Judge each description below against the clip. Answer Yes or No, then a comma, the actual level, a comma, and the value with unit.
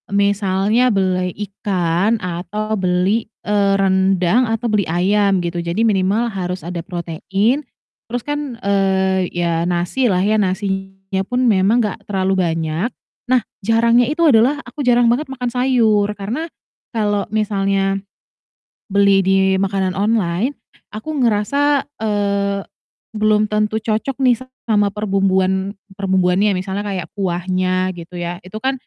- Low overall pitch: No, high, 200 Hz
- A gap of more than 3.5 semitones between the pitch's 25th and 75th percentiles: No, average, 2.9 semitones